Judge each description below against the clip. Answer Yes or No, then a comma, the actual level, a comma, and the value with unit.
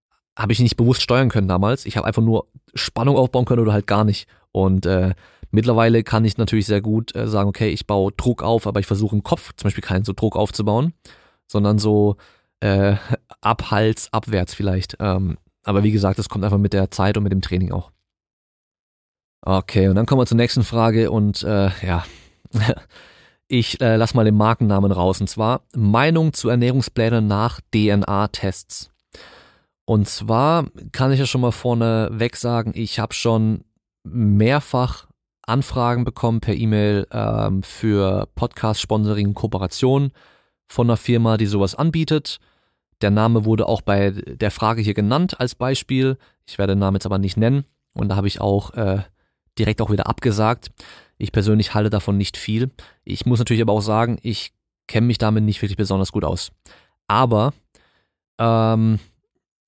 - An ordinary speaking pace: Yes, average, 170 wpm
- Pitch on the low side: Yes, low, 110 Hz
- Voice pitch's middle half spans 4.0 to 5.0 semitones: No, average, 2.8 semitones